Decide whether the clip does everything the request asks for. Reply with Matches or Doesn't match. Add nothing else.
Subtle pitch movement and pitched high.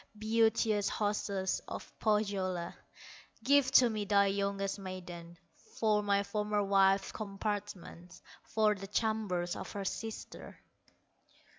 Matches